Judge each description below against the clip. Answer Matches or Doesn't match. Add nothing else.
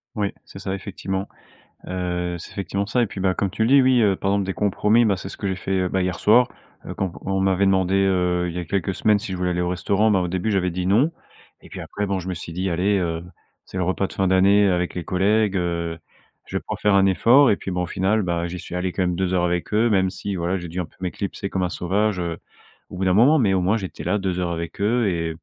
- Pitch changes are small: Matches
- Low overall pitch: Matches